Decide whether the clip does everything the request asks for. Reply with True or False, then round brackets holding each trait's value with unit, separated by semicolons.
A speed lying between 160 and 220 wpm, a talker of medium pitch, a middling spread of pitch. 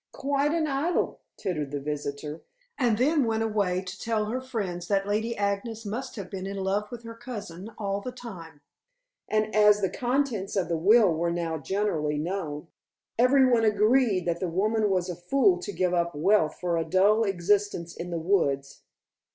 False (185 wpm; 200 Hz; 4.6 semitones)